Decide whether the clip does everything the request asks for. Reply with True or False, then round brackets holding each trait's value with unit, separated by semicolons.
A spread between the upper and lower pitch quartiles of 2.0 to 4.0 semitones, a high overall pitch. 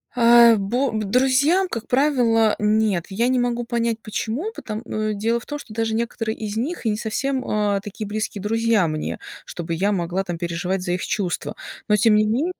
True (2.7 semitones; 220 Hz)